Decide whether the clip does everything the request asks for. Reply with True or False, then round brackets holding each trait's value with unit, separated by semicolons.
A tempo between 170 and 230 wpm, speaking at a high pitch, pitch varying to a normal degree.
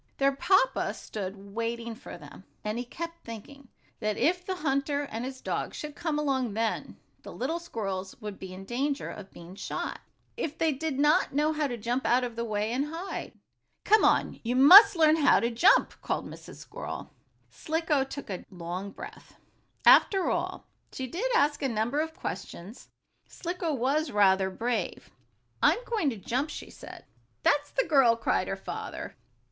False (175 wpm; 265 Hz; 5.9 semitones)